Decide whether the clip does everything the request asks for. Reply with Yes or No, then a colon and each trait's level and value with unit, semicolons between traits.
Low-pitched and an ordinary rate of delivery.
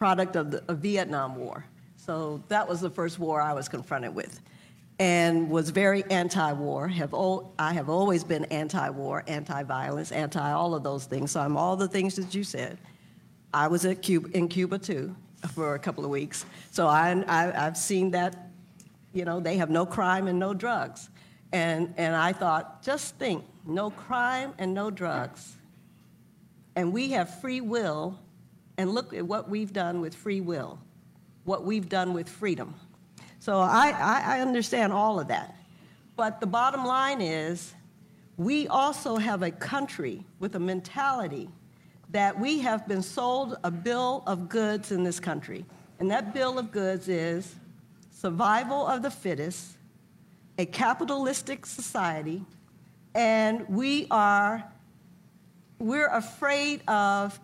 No: medium, 185 Hz; average, 160 wpm